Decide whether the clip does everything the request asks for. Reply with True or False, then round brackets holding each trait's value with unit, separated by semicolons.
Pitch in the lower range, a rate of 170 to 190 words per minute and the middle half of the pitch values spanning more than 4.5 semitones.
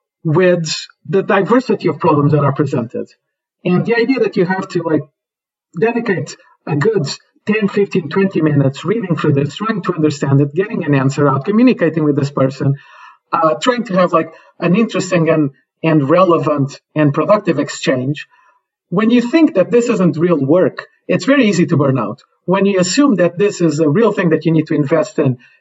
False (170 Hz; 185 wpm; 4.9 semitones)